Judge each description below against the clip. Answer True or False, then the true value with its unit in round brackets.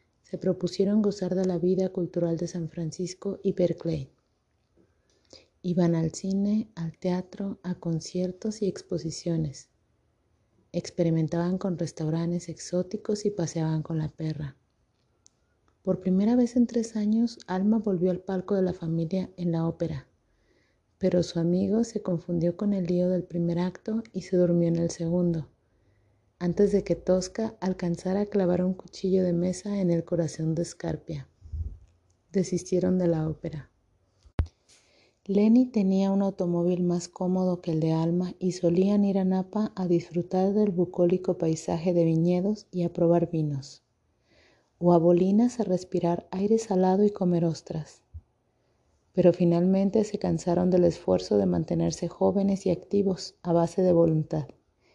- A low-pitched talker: False (175 Hz)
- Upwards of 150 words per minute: False (145 wpm)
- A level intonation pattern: True (2.3 semitones)